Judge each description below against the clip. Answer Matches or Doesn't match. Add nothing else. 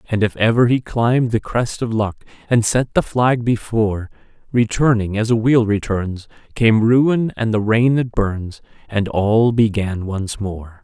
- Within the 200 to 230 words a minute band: Doesn't match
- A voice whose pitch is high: Doesn't match